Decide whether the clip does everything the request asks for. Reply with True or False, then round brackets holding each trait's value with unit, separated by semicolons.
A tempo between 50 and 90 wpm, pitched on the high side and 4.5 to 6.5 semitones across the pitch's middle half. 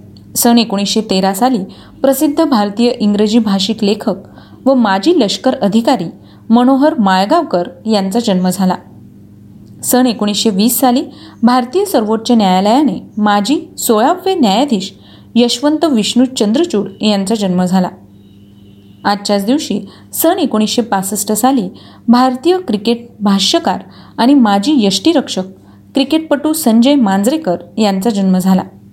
False (110 wpm; 225 Hz; 5.1 semitones)